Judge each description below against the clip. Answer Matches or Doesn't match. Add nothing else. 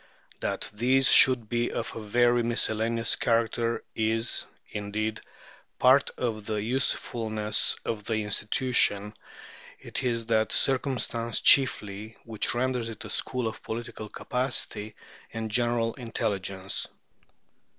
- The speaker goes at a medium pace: Doesn't match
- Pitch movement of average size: Doesn't match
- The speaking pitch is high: Doesn't match